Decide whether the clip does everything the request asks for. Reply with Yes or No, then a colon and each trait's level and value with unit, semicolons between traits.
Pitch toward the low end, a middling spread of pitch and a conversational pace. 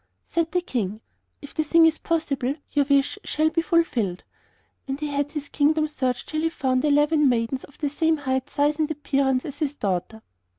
No: very high, 290 Hz; average, 3.1 semitones; average, 195 wpm